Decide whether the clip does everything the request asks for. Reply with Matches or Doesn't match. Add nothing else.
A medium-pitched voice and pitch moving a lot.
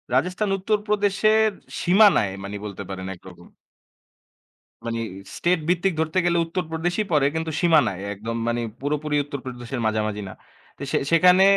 Matches